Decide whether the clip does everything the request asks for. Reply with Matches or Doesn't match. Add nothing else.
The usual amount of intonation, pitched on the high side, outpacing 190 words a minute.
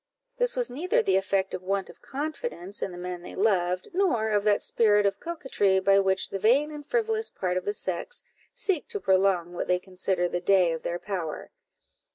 Doesn't match